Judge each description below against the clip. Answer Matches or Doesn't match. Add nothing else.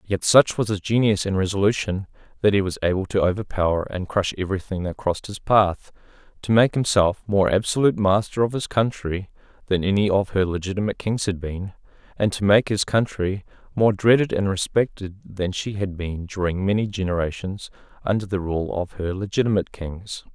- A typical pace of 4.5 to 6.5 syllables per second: Matches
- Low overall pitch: Matches